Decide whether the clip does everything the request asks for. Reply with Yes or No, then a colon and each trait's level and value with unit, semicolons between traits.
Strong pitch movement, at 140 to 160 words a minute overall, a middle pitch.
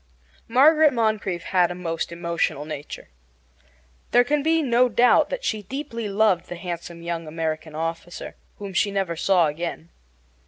Yes: wide, 5.8 semitones; average, 150 wpm; medium, 180 Hz